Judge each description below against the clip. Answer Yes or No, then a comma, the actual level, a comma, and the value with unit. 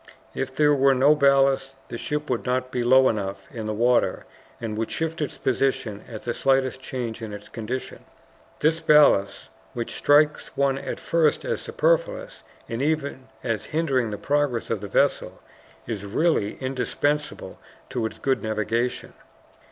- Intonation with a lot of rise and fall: No, average, 4.5 semitones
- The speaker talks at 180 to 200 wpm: No, average, 160 wpm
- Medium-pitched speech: No, low, 130 Hz